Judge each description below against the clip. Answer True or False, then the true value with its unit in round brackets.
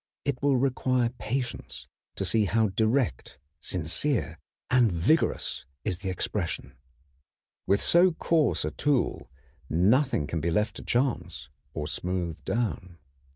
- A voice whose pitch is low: True (110 Hz)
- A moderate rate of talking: False (125 wpm)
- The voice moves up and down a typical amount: False (6.8 semitones)